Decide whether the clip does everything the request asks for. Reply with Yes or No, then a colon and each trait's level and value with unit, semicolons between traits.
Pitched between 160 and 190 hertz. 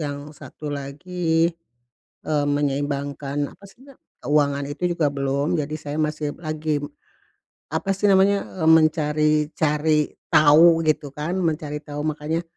No: medium, 150 Hz